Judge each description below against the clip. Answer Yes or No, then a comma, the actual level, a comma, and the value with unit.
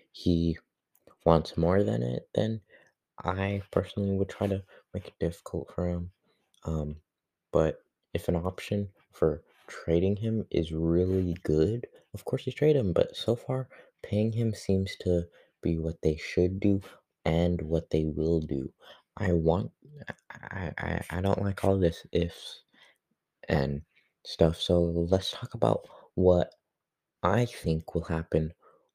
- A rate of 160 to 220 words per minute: No, average, 145 wpm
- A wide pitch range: No, average, 3.2 semitones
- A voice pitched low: Yes, very low, 85 Hz